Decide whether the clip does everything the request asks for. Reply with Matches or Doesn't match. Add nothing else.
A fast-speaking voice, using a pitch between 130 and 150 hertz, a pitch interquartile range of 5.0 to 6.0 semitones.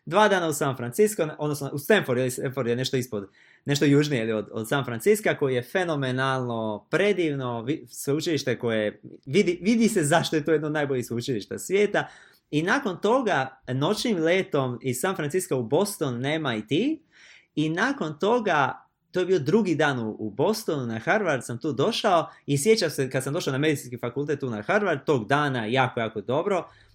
Matches